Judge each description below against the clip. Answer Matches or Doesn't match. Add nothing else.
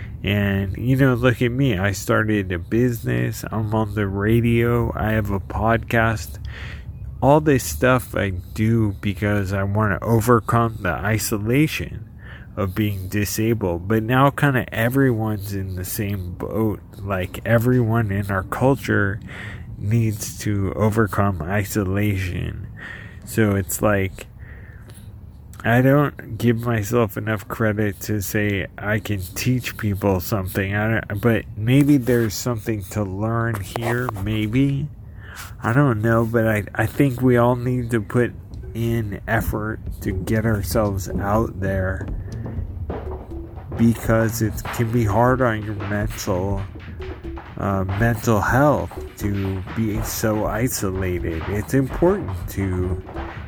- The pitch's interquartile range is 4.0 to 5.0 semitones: Doesn't match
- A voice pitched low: Matches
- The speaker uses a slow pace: Matches